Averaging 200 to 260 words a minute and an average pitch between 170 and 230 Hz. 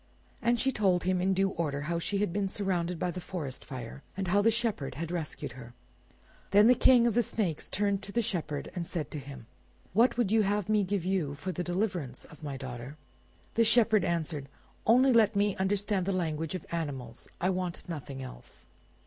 Yes: fast, 205 wpm; medium, 185 Hz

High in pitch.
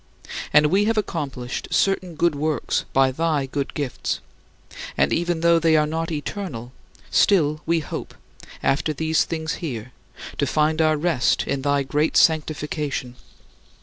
No: medium, 155 Hz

